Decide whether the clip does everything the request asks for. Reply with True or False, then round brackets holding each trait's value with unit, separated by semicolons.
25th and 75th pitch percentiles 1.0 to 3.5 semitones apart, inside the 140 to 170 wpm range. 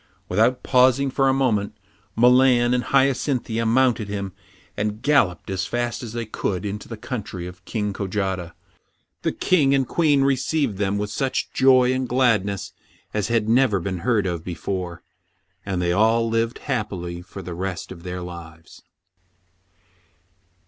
False (5.0 semitones; 150 wpm)